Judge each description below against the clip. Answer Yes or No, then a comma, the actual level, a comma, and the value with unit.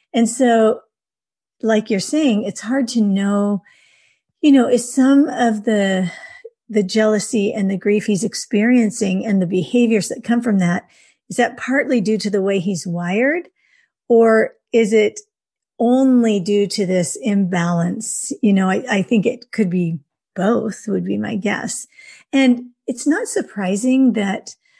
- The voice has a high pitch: Yes, high, 220 Hz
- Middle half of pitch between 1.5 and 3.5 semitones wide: No, average, 4.0 semitones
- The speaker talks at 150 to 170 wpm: Yes, average, 155 wpm